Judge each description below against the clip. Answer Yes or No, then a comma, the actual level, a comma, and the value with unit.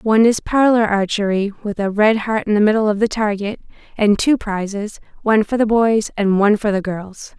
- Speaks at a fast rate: Yes, fast, 210 wpm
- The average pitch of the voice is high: Yes, high, 210 Hz